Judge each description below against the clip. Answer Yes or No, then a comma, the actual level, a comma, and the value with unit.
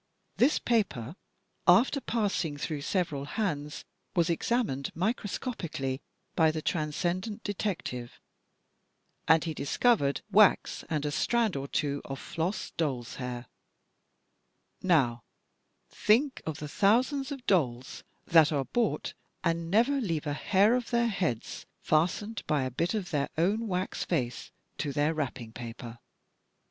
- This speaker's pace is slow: Yes, slow, 130 wpm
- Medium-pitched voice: Yes, medium, 165 Hz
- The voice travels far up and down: Yes, wide, 6.9 semitones